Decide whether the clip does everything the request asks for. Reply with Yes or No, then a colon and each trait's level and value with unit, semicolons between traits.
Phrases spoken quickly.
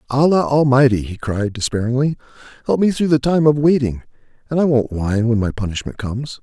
No: average, 185 wpm